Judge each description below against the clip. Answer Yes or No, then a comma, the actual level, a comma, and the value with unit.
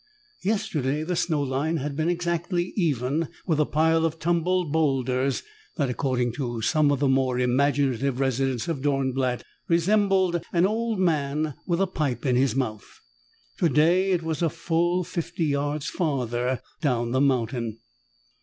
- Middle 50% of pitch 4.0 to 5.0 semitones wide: Yes, average, 4.4 semitones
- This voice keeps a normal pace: Yes, average, 150 wpm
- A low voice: No, medium, 145 Hz